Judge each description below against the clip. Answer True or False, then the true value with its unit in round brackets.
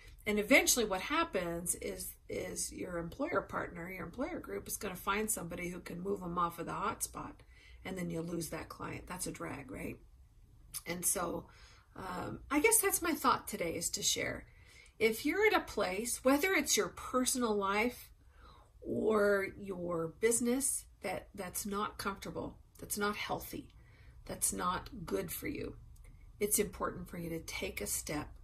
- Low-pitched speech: False (200 Hz)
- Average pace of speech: True (175 wpm)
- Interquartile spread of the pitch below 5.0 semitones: False (5.6 semitones)